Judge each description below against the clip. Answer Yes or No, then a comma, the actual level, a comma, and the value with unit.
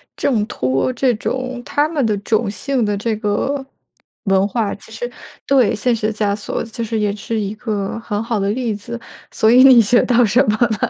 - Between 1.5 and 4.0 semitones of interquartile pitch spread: Yes, average, 2.9 semitones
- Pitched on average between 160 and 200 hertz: No, high, 225 Hz